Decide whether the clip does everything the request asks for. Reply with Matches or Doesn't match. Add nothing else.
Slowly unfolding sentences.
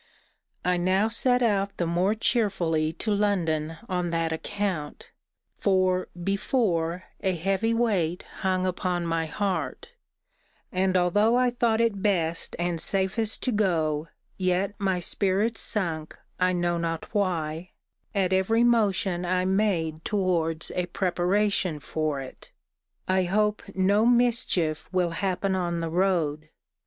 Matches